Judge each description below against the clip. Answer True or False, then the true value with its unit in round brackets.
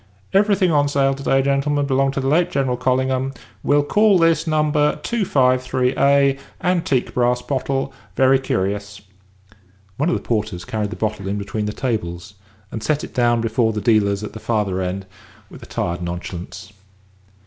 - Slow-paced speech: False (165 wpm)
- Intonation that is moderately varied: True (5.0 semitones)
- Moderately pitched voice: False (130 Hz)